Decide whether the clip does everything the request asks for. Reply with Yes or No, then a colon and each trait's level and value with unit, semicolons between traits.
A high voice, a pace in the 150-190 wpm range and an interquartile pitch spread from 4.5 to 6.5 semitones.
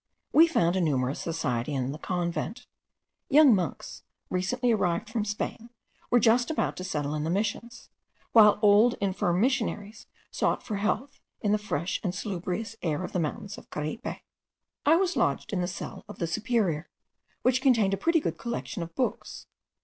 Yes: high, 205 Hz; average, 170 wpm; wide, 5.5 semitones